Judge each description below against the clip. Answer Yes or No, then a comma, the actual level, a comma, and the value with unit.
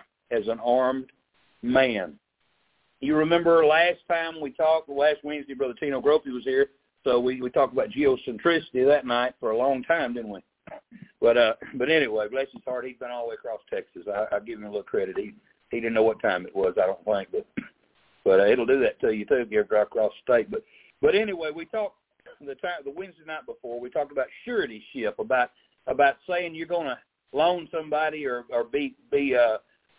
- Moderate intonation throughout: No, wide, 7.1 semitones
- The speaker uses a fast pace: Yes, fast, 215 wpm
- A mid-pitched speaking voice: Yes, medium, 155 Hz